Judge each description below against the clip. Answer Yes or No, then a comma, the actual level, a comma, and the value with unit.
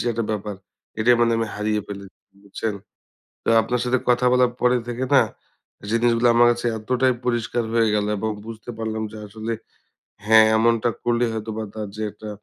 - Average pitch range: No, narrow, 1.8 semitones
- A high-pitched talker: No, low, 115 Hz